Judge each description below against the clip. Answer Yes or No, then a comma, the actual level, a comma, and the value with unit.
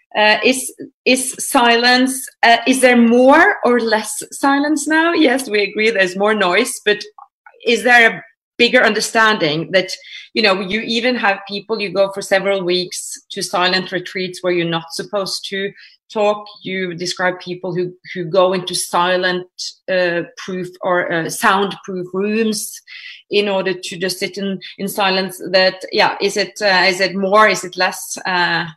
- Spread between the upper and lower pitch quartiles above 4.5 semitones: No, average, 3.5 semitones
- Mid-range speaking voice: No, high, 195 Hz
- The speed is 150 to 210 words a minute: Yes, average, 165 wpm